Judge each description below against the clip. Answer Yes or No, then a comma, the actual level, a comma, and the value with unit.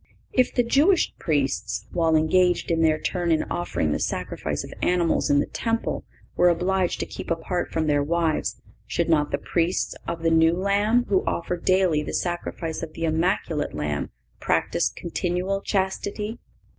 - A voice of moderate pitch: Yes, medium, 170 Hz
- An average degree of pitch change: Yes, average, 3.1 semitones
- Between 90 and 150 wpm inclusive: No, average, 165 wpm